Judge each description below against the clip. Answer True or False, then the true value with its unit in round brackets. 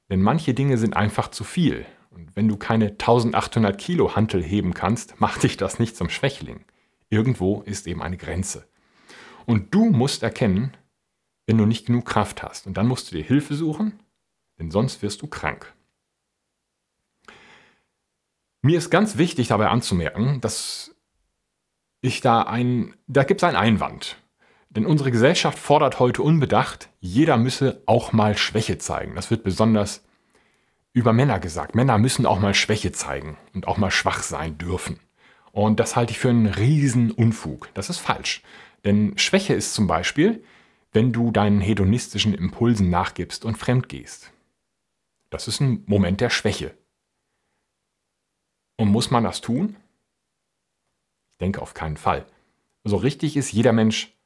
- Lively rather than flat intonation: False (4.2 semitones)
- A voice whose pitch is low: True (115 Hz)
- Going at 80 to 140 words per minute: False (155 wpm)